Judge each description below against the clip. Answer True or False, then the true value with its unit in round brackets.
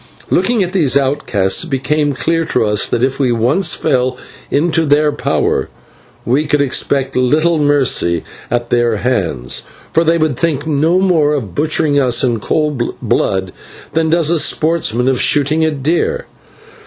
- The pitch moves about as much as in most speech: True (4.3 semitones)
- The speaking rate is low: False (160 wpm)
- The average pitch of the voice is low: False (145 Hz)